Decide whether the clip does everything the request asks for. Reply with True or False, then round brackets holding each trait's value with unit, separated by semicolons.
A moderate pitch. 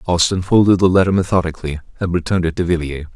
False (90 Hz)